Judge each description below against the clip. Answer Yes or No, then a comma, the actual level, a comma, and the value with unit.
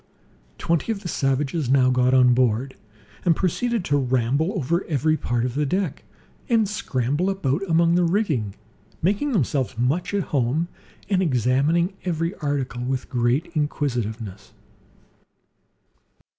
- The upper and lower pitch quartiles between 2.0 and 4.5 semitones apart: No, wide, 5.6 semitones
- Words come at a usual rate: No, slow, 130 wpm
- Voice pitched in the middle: Yes, medium, 145 Hz